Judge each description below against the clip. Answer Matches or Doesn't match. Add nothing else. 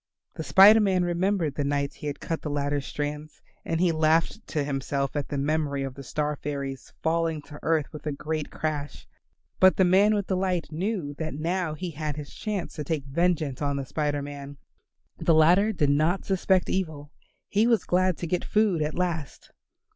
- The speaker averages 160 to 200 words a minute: Matches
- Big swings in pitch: Doesn't match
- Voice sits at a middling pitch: Matches